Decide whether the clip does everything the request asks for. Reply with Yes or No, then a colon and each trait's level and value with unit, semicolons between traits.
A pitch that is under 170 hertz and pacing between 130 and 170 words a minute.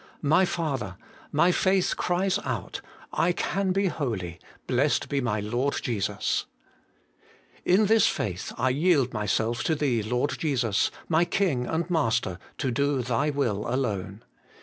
Yes: low, 135 Hz; average, 140 wpm